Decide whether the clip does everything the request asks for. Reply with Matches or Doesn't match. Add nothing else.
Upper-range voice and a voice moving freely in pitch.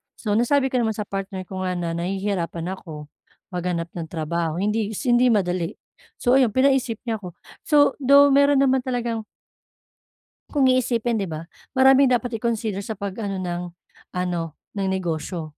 Matches